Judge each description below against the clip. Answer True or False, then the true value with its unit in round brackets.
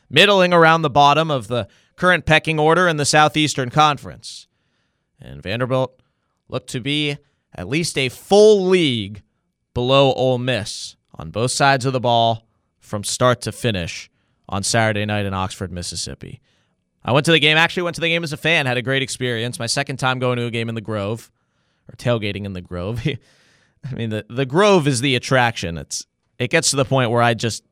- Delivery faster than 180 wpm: True (195 wpm)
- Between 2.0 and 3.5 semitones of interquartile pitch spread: False (4.6 semitones)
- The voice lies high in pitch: False (130 Hz)